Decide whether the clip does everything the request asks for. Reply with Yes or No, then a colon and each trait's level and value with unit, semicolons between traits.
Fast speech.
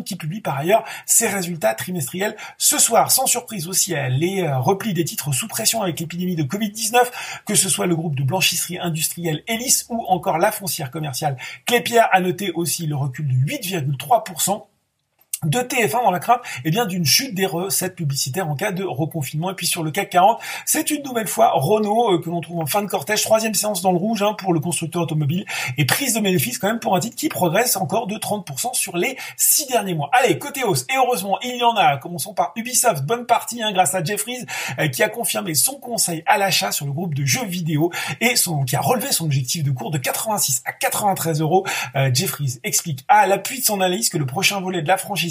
Yes: fast, 225 wpm